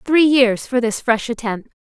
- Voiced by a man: No, female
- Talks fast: No, average, 195 wpm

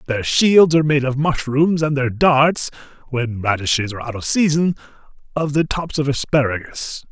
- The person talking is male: Yes, male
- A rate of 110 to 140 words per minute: No, average, 170 wpm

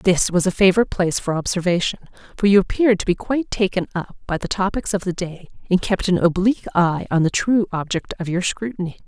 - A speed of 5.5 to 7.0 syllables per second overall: Yes, 6.3 syllables/s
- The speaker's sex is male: No, female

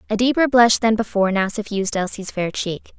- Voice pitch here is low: No, high, 210 Hz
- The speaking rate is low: No, average, 200 wpm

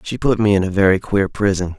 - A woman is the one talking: No, male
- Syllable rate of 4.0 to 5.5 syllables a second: No, 5.9 syllables/s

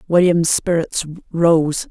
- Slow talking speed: Yes, slow, 95 wpm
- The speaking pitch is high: No, medium, 170 Hz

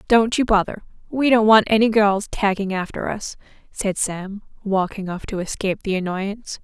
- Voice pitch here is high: Yes, high, 205 Hz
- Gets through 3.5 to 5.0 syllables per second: Yes, 4.9 syllables/s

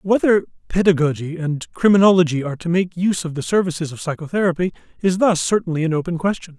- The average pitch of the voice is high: No, medium, 170 Hz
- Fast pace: No, average, 175 wpm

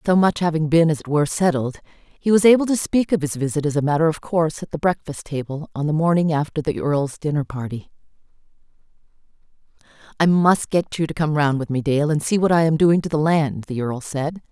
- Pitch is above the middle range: No, medium, 155 Hz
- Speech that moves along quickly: Yes, fast, 225 wpm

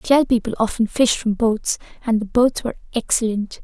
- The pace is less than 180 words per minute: No, average, 200 wpm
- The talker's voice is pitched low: No, high, 230 Hz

